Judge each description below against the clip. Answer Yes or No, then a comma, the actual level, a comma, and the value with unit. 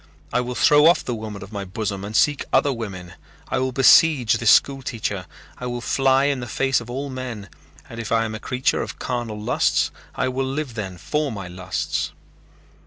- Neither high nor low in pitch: No, low, 120 Hz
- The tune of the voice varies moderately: Yes, average, 4.0 semitones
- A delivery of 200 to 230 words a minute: Yes, fast, 205 wpm